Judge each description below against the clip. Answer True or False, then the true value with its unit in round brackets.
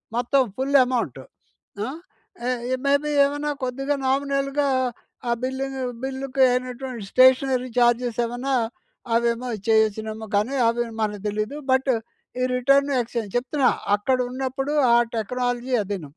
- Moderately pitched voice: False (255 Hz)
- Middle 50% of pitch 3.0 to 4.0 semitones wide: False (2.6 semitones)